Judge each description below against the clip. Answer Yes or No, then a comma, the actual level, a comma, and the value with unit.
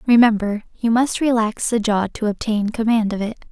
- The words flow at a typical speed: Yes, average, 190 wpm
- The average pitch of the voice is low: No, high, 225 Hz